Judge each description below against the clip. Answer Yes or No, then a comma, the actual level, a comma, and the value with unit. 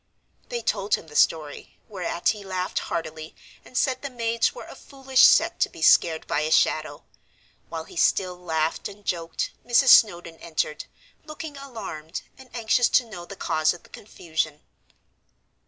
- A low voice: No, medium, 180 Hz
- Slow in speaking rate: No, average, 165 wpm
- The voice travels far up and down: Yes, wide, 6.6 semitones